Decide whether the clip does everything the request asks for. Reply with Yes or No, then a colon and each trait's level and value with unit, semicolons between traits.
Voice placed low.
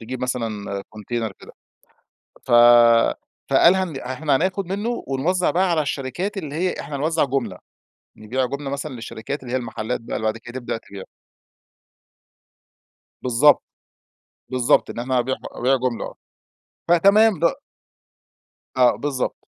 Yes: low, 130 Hz